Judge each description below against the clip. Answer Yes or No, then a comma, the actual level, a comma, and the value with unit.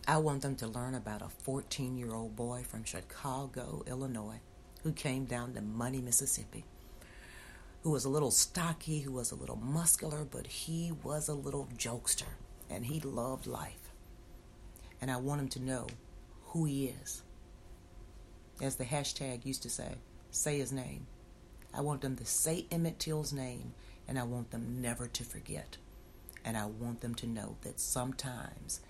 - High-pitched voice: No, low, 130 Hz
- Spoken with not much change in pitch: No, average, 3.3 semitones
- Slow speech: No, average, 165 wpm